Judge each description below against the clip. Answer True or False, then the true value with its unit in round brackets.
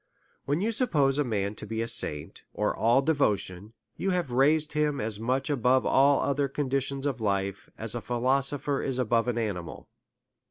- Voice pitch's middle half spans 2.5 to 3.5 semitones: False (4.2 semitones)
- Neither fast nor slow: True (175 wpm)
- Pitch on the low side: True (130 Hz)